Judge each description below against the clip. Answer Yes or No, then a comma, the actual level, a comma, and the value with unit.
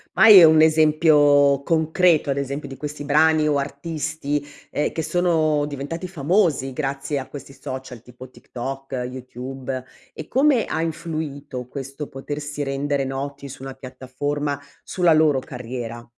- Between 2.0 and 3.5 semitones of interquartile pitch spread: Yes, narrow, 2.6 semitones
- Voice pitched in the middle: Yes, medium, 145 Hz